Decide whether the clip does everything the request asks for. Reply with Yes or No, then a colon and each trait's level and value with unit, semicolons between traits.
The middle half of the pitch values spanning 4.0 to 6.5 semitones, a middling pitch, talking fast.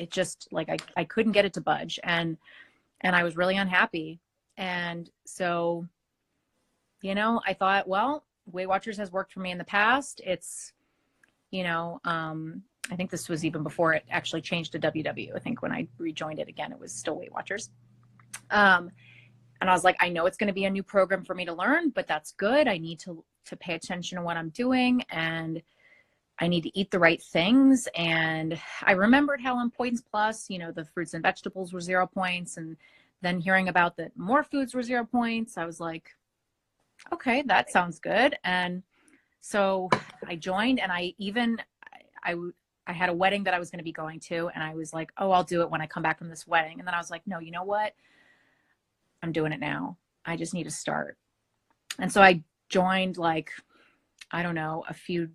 No: average, 3.2 semitones; medium, 180 Hz; fast, 210 wpm